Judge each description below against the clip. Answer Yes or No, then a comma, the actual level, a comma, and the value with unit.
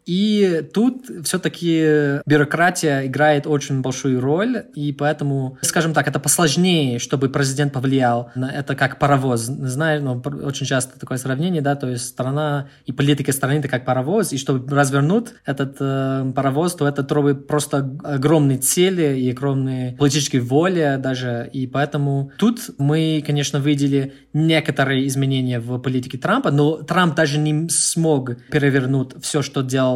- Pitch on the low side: No, medium, 145 Hz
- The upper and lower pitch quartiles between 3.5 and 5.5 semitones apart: No, narrow, 2.4 semitones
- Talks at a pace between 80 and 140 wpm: No, average, 150 wpm